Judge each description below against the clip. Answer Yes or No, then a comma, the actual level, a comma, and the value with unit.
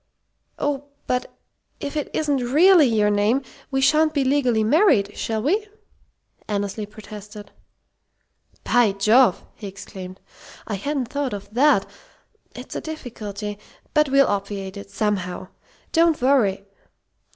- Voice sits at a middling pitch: No, high, 230 Hz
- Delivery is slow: Yes, slow, 125 wpm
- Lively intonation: Yes, wide, 5.8 semitones